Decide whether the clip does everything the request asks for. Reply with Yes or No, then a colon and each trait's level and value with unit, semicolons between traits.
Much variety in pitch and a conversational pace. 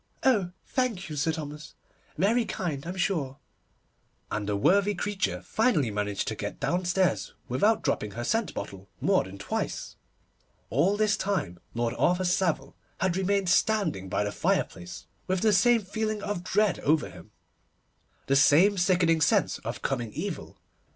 Yes: wide, 6.9 semitones; average, 150 wpm